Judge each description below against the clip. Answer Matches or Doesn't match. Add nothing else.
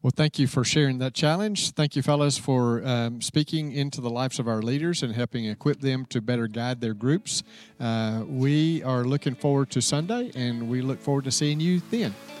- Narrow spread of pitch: Doesn't match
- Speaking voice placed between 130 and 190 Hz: Matches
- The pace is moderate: Doesn't match